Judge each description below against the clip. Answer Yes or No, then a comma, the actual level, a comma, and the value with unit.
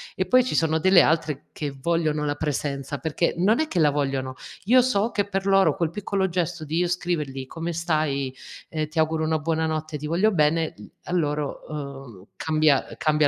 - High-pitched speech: No, medium, 160 Hz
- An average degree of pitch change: Yes, average, 3.1 semitones